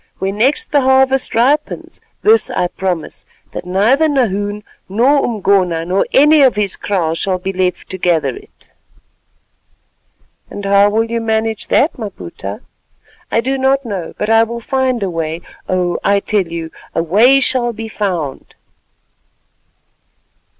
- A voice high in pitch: Yes, high, 210 Hz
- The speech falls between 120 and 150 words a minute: Yes, average, 145 wpm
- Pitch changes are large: Yes, wide, 5.9 semitones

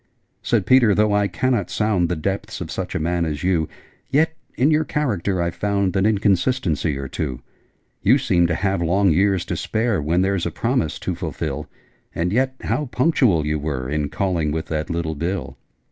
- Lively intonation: No, average, 5.0 semitones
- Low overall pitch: Yes, very low, 95 Hz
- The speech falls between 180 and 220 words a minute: Yes, average, 190 wpm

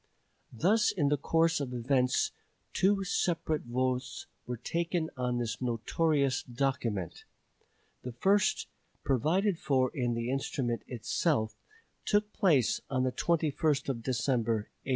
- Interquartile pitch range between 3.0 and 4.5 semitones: No, average, 5.0 semitones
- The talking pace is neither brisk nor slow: No, slow, 125 wpm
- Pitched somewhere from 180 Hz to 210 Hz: No, low, 135 Hz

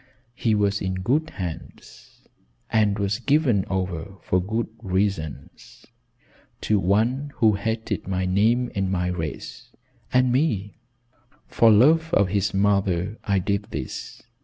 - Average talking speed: No, slow, 130 wpm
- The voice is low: Yes, low, 100 Hz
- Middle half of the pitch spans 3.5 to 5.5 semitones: Yes, average, 3.8 semitones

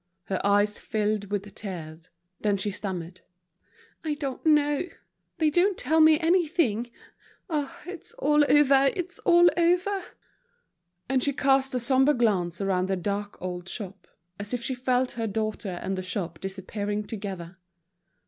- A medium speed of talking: Yes, average, 150 wpm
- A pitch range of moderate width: No, wide, 7.2 semitones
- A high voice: Yes, high, 225 Hz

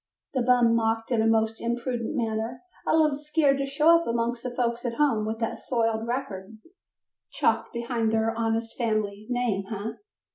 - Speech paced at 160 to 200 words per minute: Yes, average, 175 wpm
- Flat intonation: Yes, narrow, 2.0 semitones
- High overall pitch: Yes, high, 235 Hz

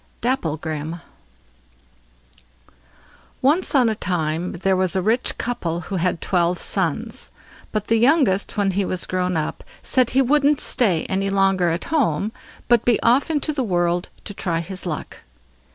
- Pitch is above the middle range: Yes, high, 195 Hz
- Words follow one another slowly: No, average, 150 wpm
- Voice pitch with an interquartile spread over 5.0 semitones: Yes, wide, 5.6 semitones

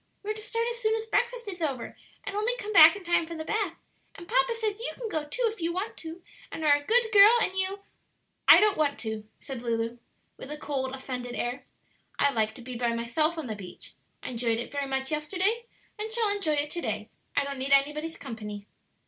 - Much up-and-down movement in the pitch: Yes, wide, 8.3 semitones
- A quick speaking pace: Yes, fast, 235 wpm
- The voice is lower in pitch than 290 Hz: No, very high, 315 Hz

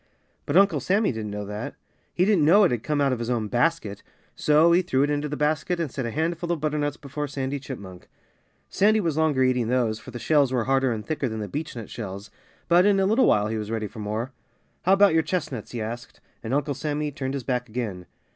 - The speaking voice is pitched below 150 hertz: Yes, low, 135 Hz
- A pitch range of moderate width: No, wide, 5.7 semitones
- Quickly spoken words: Yes, fast, 235 wpm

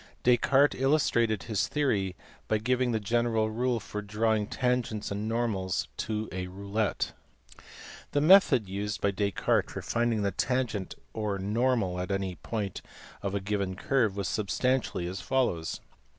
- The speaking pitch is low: Yes, low, 110 Hz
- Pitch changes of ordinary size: Yes, average, 3.6 semitones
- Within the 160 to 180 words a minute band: No, average, 145 wpm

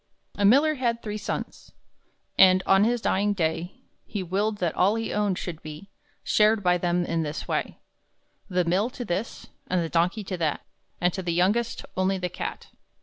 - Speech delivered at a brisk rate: No, average, 185 wpm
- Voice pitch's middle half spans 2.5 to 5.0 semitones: Yes, average, 3.2 semitones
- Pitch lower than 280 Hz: Yes, high, 190 Hz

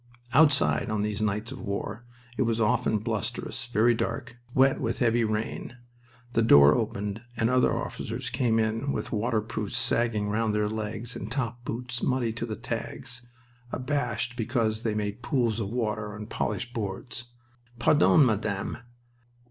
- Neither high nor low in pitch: No, low, 115 Hz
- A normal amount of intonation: No, narrow, 2.2 semitones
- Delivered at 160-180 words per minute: No, average, 150 wpm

